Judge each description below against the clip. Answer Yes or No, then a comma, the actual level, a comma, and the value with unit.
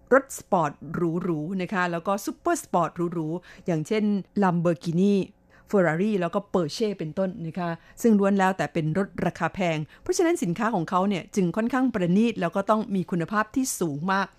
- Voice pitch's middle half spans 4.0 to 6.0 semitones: No, average, 3.4 semitones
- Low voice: No, medium, 185 Hz